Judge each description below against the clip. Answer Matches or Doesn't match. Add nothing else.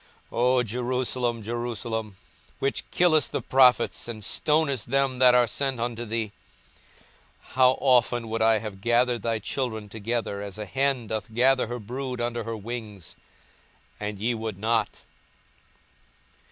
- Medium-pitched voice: Doesn't match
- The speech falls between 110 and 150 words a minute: Matches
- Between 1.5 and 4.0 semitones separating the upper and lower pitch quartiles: Matches